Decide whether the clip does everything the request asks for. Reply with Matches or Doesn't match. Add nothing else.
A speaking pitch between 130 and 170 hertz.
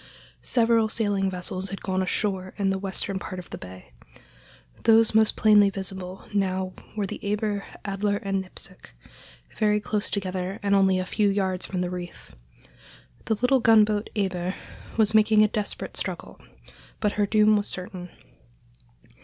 Doesn't match